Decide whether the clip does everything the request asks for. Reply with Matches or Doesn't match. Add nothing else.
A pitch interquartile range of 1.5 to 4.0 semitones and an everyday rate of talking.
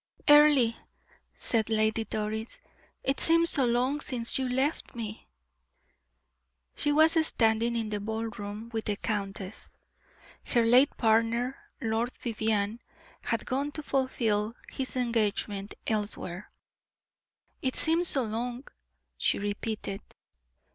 Doesn't match